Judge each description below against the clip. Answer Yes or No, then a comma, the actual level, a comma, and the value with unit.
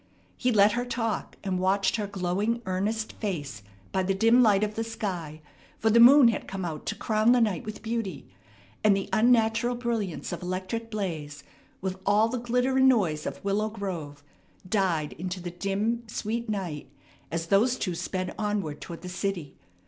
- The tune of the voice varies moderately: Yes, average, 3.8 semitones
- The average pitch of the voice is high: Yes, high, 200 Hz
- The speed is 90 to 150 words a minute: No, average, 180 wpm